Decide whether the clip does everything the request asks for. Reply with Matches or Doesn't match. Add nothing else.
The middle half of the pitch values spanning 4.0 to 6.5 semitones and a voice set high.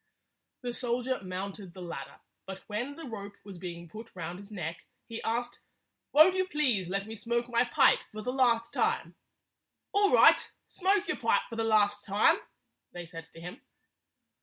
Matches